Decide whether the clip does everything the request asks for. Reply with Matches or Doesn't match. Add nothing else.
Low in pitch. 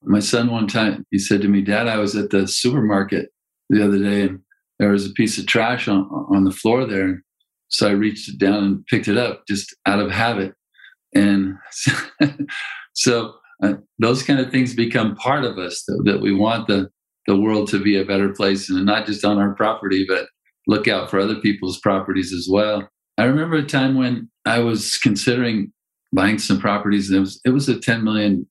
Matches